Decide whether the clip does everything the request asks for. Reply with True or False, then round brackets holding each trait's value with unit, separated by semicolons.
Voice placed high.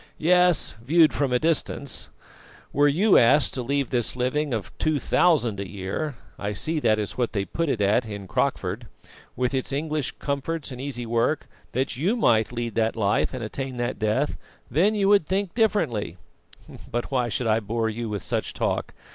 False (125 Hz)